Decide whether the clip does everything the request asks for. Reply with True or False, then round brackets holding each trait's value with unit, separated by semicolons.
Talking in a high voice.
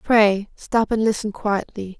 True (210 Hz)